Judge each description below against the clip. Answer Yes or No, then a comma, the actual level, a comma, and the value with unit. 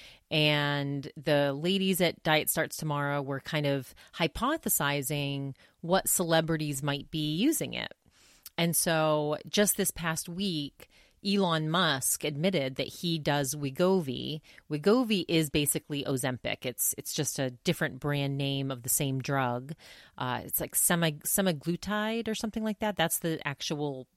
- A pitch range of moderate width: Yes, average, 3.7 semitones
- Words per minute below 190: Yes, average, 140 wpm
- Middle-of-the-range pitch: Yes, medium, 155 Hz